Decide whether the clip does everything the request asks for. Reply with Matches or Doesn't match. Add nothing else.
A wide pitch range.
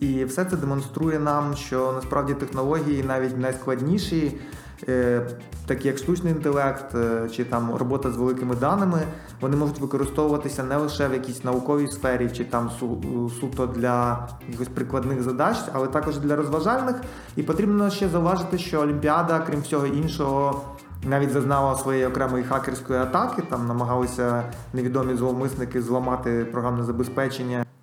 Doesn't match